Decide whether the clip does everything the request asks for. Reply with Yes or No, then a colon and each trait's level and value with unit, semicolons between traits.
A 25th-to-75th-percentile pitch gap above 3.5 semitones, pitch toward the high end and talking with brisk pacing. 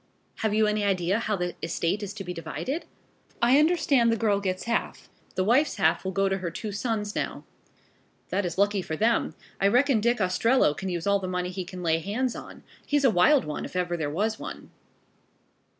Yes: average, 4.2 semitones; high, 200 Hz; fast, 210 wpm